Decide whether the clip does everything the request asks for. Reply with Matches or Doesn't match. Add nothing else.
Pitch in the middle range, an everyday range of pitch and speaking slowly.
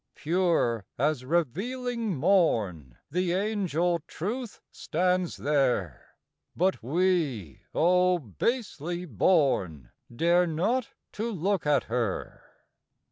Doesn't match